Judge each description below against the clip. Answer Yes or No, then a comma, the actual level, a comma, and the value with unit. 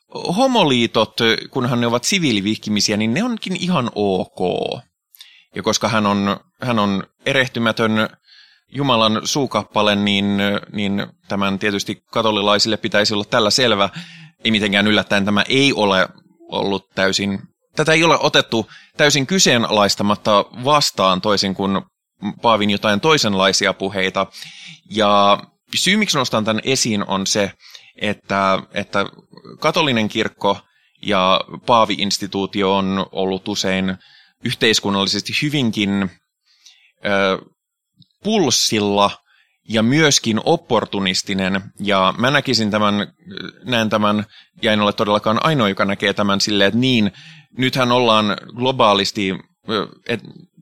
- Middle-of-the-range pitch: No, low, 105 Hz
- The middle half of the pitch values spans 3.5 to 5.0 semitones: Yes, average, 4.0 semitones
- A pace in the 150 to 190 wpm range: No, average, 110 wpm